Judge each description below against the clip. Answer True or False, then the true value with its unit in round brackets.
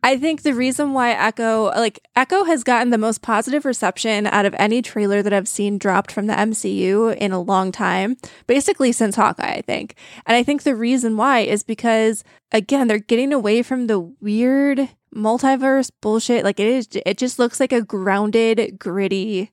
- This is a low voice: False (225 Hz)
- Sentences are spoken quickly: False (190 wpm)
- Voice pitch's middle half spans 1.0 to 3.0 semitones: False (3.5 semitones)